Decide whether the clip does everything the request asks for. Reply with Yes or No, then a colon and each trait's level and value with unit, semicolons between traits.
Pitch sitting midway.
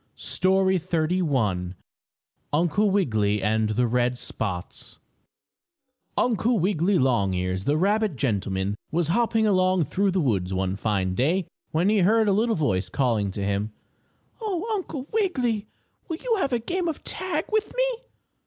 Yes: medium, 170 Hz